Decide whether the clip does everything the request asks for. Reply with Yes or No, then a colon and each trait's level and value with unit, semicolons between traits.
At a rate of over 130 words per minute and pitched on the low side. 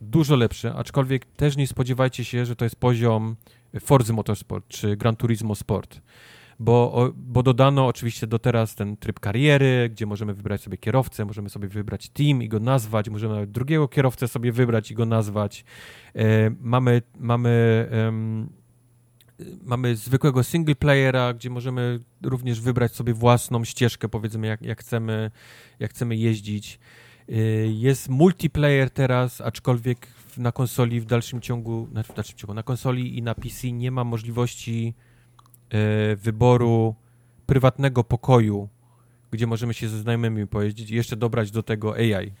Yes: average, 140 wpm; low, 120 Hz